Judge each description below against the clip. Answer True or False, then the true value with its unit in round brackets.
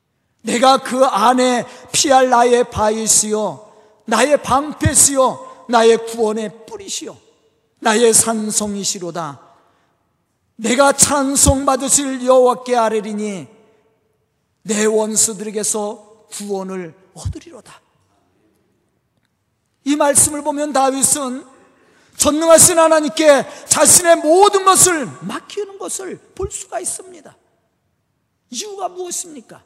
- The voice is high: True (250 Hz)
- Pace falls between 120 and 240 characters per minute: True (225 characters per minute)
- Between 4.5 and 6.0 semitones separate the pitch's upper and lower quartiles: True (5.6 semitones)